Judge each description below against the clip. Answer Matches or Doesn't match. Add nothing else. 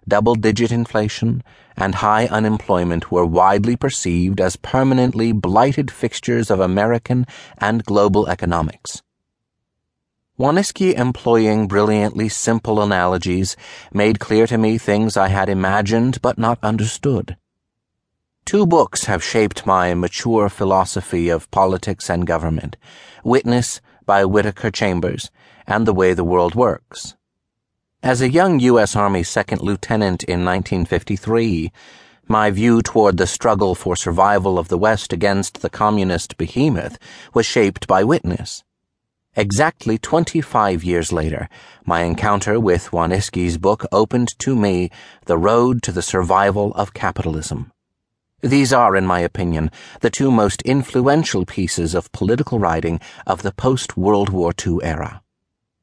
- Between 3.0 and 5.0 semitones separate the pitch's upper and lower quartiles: Matches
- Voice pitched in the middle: Doesn't match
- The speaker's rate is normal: Doesn't match